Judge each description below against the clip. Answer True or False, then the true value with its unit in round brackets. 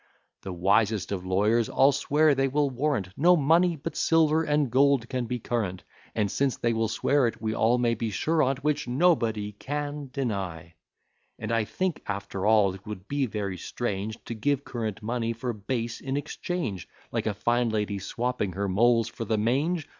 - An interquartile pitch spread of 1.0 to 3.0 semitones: False (5.1 semitones)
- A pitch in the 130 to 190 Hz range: False (115 Hz)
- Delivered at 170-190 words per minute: True (180 wpm)